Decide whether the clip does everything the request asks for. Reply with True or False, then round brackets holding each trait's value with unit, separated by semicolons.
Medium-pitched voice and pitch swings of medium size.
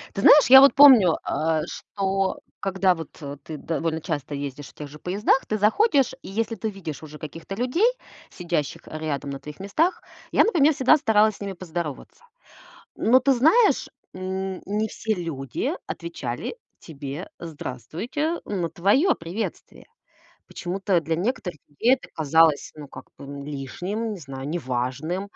False (180 Hz; 6.3 semitones)